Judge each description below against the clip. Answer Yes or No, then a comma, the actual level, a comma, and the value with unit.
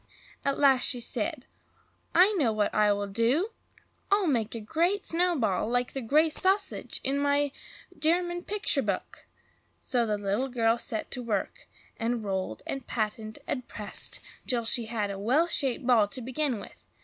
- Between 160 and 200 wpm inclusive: Yes, average, 165 wpm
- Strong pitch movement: Yes, wide, 5.9 semitones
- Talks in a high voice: Yes, high, 245 Hz